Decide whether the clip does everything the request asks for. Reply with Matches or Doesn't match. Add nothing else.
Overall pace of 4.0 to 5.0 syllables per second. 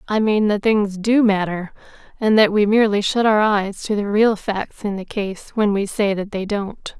Matches